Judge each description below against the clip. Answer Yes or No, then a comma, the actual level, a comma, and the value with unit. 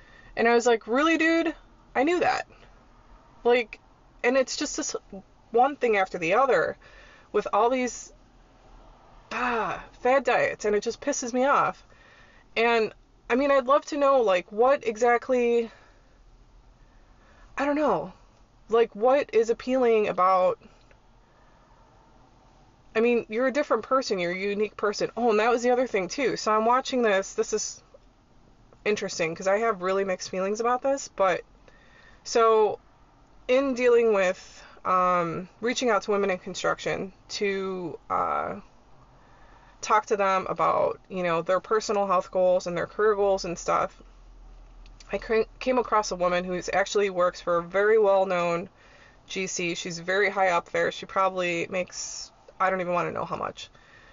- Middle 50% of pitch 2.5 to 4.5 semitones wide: No, average, 5.0 semitones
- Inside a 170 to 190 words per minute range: No, average, 155 wpm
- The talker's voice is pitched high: Yes, high, 210 Hz